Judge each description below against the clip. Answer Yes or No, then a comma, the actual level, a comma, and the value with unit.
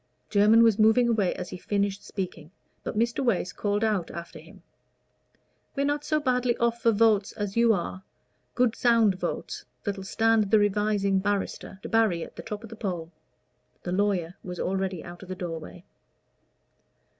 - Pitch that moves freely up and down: No, average, 3.3 semitones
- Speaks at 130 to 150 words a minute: No, average, 165 wpm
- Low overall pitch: No, high, 205 Hz